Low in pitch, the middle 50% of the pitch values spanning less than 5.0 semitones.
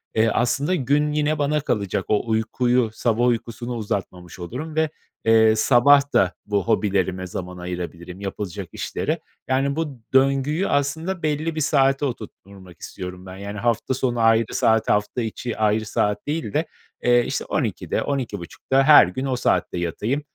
No: low, 120 Hz; wide, 5.5 semitones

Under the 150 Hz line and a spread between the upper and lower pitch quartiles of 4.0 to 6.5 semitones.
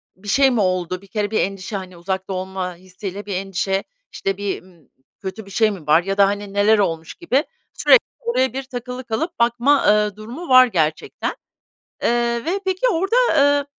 No: high, 205 Hz; average, 5.2 semitones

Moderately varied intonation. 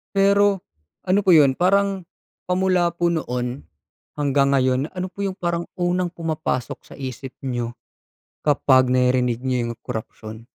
No: wide, 6.2 semitones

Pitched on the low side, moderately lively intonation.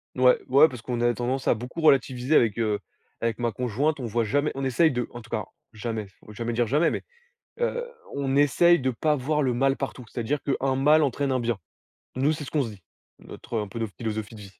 Yes: low, 125 Hz; average, 3.4 semitones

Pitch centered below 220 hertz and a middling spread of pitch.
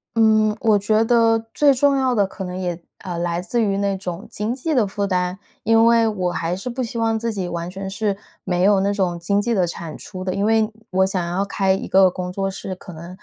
Yes: high, 195 Hz; average, 3.5 semitones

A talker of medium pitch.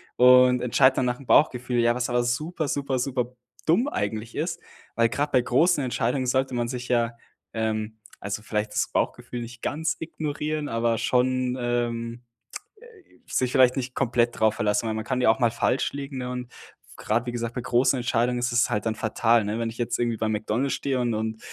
No: low, 120 Hz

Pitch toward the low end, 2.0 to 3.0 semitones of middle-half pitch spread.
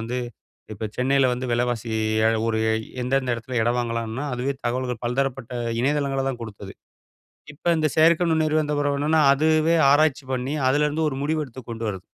No: low, 130 Hz; average, 3.8 semitones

